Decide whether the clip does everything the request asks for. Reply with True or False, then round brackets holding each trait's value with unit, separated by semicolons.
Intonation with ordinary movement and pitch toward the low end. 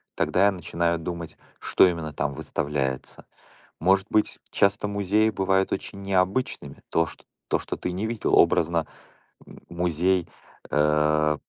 True (3.8 semitones; 90 Hz)